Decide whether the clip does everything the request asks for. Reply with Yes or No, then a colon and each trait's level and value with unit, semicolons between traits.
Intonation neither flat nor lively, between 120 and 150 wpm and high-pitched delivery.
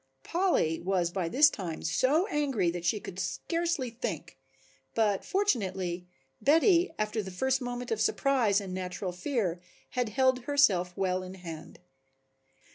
No: wide, 6.7 semitones; average, 140 wpm; high, 210 Hz